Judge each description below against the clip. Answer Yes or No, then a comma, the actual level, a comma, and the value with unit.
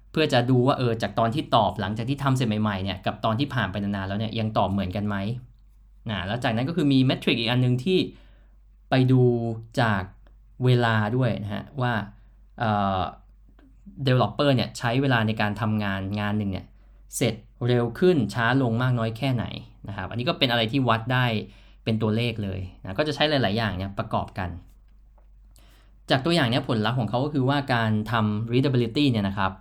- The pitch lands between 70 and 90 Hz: No, low, 115 Hz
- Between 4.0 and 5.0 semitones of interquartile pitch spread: No, average, 3.4 semitones